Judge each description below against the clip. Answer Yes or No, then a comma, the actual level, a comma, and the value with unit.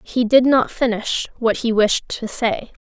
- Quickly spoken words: No, average, 190 wpm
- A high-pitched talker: Yes, high, 235 Hz